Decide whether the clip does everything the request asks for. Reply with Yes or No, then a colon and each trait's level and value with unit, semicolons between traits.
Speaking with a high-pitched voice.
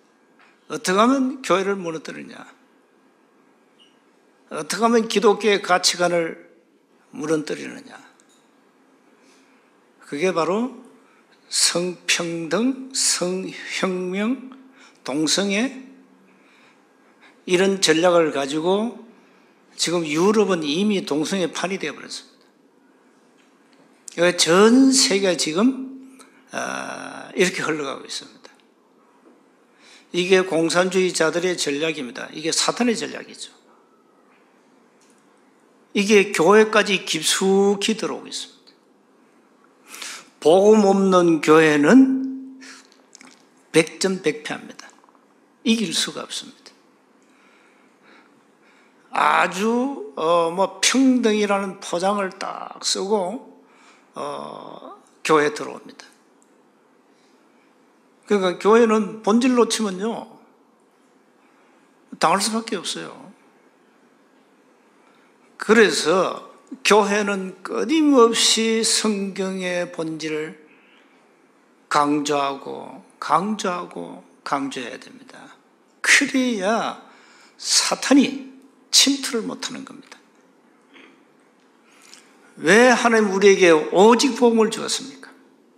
Yes: high, 205 Hz